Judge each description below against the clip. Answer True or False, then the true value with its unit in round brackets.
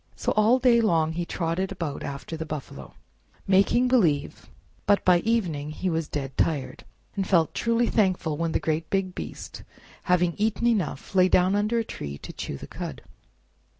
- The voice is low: False (180 Hz)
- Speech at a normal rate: True (175 wpm)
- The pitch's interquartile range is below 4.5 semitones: False (4.9 semitones)